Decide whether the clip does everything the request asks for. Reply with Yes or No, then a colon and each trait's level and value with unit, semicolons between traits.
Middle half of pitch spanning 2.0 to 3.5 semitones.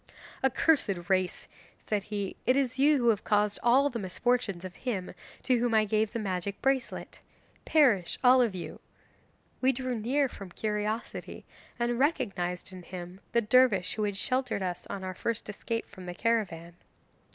No: average, 4.8 semitones